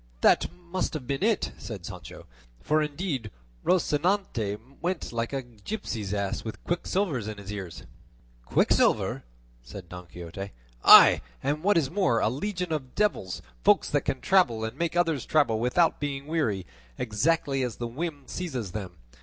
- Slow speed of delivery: No, average, 155 wpm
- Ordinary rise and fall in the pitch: No, wide, 7.8 semitones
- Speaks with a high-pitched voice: No, low, 135 Hz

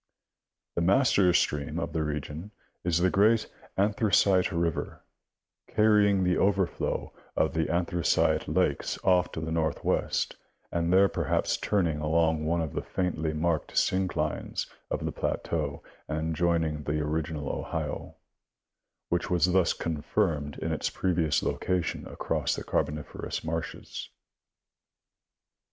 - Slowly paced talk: Yes, slow, 125 wpm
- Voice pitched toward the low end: Yes, very low, 85 Hz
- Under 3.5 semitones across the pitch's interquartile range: Yes, average, 2.9 semitones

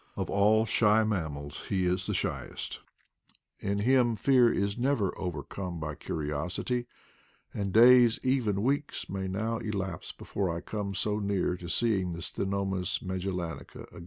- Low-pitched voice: Yes, low, 100 Hz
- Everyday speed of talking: Yes, average, 155 wpm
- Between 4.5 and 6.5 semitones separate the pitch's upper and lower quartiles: No, average, 3.5 semitones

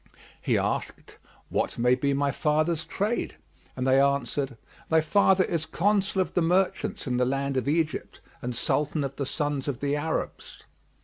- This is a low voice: No, medium, 145 Hz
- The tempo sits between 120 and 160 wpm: No, average, 170 wpm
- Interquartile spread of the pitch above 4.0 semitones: No, average, 3.4 semitones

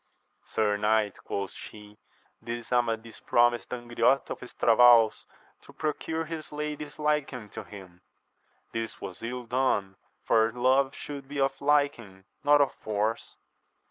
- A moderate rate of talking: No, slow, 130 wpm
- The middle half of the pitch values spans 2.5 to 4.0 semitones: No, average, 4.4 semitones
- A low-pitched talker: Yes, low, 120 Hz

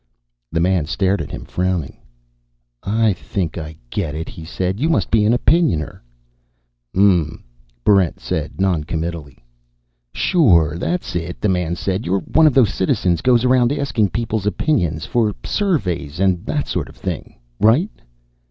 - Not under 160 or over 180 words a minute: No, average, 150 wpm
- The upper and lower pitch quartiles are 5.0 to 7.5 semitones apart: Yes, wide, 5.4 semitones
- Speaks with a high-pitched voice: No, very low, 95 Hz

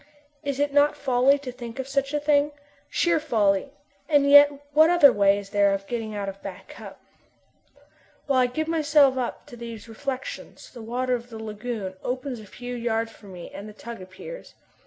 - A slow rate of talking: No, average, 195 wpm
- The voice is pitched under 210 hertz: No, high, 245 Hz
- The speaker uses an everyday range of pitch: Yes, average, 4.6 semitones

